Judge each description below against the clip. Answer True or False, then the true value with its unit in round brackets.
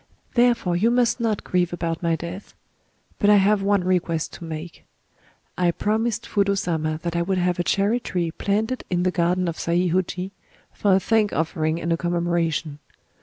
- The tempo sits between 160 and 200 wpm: True (175 wpm)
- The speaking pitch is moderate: True (180 Hz)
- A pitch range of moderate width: True (3.2 semitones)